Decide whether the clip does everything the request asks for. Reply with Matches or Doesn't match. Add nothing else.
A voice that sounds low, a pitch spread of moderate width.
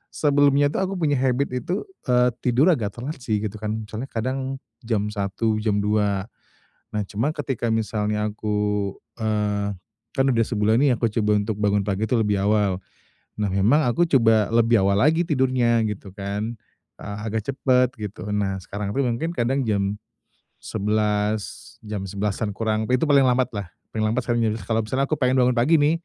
Matches